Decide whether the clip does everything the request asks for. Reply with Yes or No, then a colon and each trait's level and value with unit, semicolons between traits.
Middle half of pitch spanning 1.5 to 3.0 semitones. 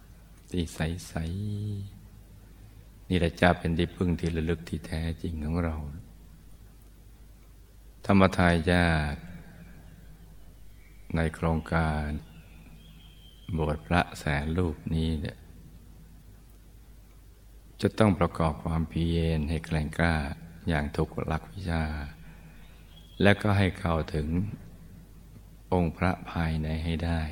Yes: narrow, 2.6 semitones